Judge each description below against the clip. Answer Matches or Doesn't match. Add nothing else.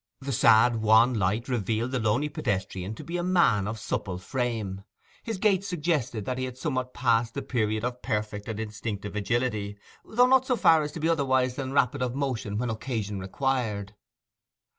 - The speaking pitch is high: Doesn't match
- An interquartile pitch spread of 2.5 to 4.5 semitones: Matches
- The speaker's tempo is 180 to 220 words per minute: Matches